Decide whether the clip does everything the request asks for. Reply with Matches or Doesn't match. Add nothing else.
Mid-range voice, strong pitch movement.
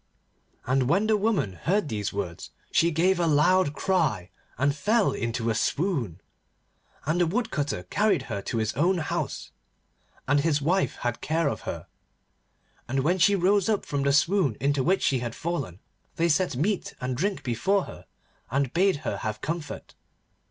Matches